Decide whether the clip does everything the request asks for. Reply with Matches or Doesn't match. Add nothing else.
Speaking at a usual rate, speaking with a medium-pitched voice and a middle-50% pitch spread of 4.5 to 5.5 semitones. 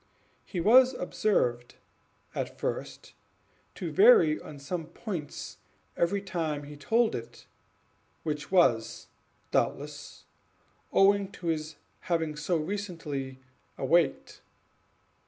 Doesn't match